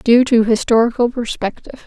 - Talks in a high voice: Yes, high, 235 Hz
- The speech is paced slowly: Yes, slow, 130 wpm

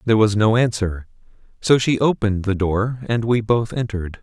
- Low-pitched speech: Yes, low, 110 Hz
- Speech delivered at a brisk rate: No, average, 185 wpm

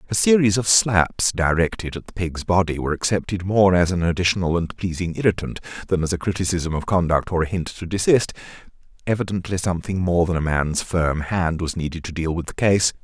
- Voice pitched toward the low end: Yes, very low, 90 Hz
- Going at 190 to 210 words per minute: Yes, fast, 205 wpm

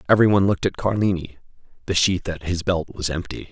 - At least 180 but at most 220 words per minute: Yes, fast, 205 wpm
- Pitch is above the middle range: No, very low, 90 Hz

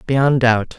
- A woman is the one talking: Yes, female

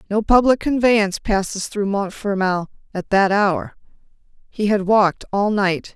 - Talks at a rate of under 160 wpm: Yes, average, 140 wpm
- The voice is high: Yes, high, 205 Hz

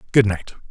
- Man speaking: Yes, male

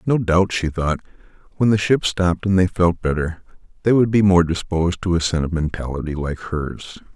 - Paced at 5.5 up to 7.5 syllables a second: No, 5.3 syllables/s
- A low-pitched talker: Yes, very low, 90 Hz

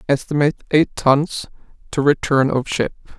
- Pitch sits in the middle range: Yes, medium, 145 Hz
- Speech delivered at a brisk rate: No, slow, 130 wpm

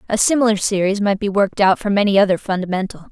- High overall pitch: Yes, high, 200 Hz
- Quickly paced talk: Yes, fast, 210 wpm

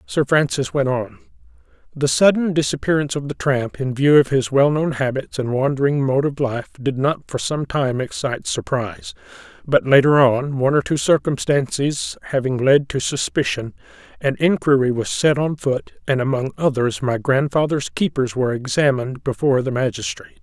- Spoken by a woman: No, male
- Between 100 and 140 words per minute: No, average, 165 wpm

